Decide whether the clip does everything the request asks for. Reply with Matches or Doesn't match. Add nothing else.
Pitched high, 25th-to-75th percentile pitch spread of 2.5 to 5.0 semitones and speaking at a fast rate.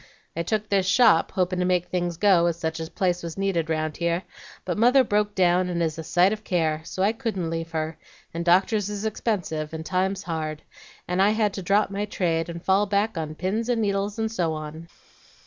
Doesn't match